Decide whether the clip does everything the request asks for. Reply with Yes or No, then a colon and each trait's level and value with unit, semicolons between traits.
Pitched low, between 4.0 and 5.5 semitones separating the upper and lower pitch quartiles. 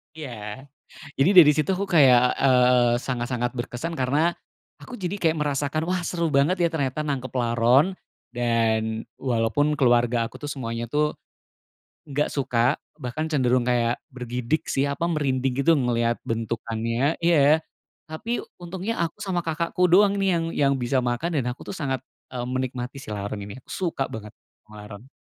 Yes: low, 130 Hz; average, 4.6 semitones